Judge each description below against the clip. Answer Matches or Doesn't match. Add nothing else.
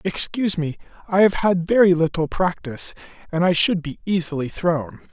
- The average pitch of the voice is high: Doesn't match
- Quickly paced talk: Doesn't match